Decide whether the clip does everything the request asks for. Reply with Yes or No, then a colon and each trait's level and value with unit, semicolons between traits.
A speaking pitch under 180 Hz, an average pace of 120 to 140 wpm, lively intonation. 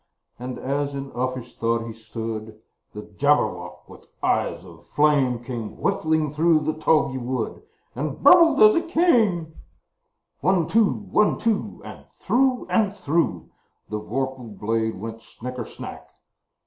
Yes: low, 135 Hz; slow, 135 wpm; wide, 6.9 semitones